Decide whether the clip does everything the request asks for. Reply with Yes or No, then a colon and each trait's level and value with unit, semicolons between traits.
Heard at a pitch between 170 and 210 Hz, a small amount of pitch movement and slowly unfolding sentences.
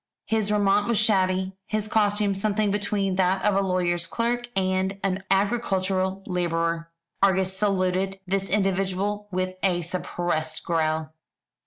Yes: high, 190 Hz; narrow, 1.8 semitones; slow, 130 wpm